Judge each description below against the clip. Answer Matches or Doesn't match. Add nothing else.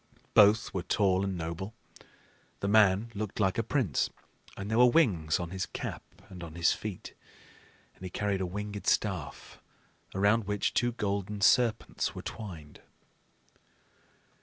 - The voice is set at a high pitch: Doesn't match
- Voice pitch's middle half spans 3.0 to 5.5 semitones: Doesn't match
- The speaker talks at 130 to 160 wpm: Matches